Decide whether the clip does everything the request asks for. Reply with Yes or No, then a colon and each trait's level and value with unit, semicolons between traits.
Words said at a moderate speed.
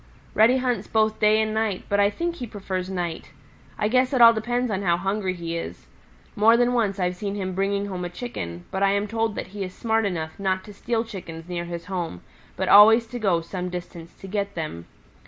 No: fast, 225 wpm